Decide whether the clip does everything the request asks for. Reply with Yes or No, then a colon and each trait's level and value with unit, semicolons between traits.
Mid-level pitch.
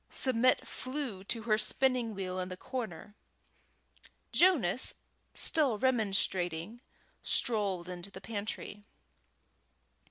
No: high, 215 Hz